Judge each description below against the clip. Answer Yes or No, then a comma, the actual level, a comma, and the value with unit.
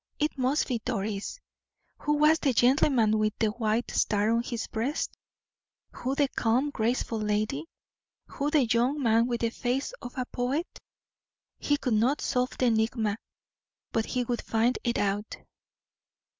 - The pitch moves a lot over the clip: No, average, 3.2 semitones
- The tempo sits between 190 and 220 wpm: No, average, 155 wpm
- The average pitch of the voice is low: No, high, 240 Hz